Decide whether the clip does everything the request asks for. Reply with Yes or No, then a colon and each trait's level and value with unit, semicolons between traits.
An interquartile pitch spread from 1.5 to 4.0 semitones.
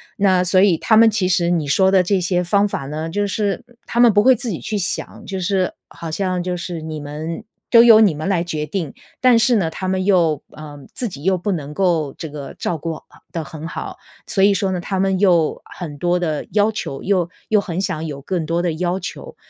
Yes: average, 3.7 semitones